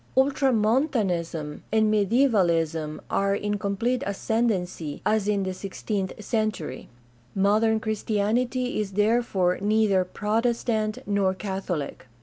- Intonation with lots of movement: No, average, 2.9 semitones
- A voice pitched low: No, high, 210 Hz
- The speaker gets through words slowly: Yes, slow, 100 wpm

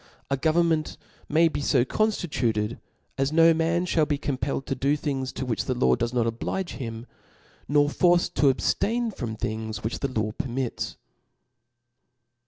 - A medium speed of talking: Yes, average, 165 wpm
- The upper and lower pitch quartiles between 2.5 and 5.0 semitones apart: No, wide, 5.5 semitones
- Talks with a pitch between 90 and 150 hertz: Yes, medium, 140 Hz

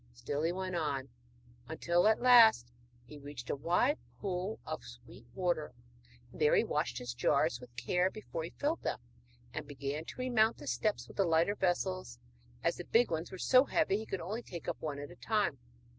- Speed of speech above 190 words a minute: Yes, average, 200 wpm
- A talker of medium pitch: Yes, medium, 170 Hz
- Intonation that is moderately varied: No, wide, 6.4 semitones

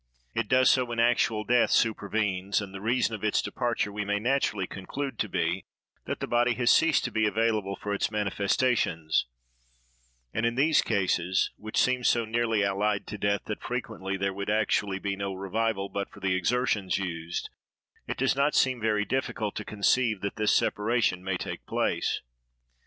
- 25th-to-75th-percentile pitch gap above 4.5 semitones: No, average, 3.3 semitones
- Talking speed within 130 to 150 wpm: No, average, 180 wpm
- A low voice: Yes, low, 105 Hz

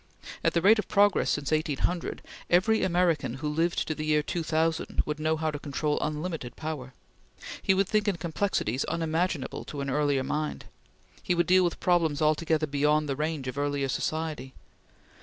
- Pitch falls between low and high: Yes, medium, 155 Hz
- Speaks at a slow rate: No, average, 175 wpm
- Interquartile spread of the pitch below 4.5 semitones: Yes, average, 2.7 semitones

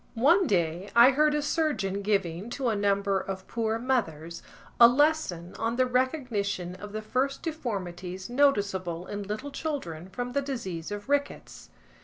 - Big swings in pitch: Yes, wide, 5.9 semitones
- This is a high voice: Yes, high, 215 Hz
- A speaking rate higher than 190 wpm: No, average, 155 wpm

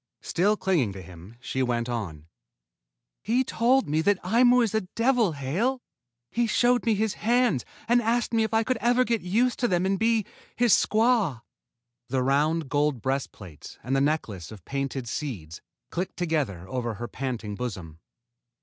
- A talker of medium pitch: Yes, medium, 165 Hz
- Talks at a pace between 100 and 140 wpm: No, average, 170 wpm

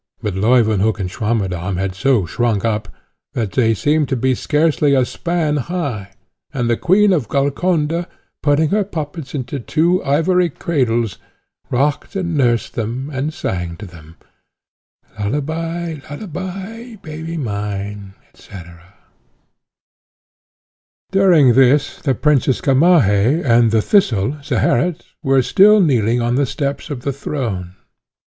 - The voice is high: No, low, 135 Hz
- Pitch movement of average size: No, wide, 6.2 semitones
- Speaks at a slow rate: Yes, slow, 125 wpm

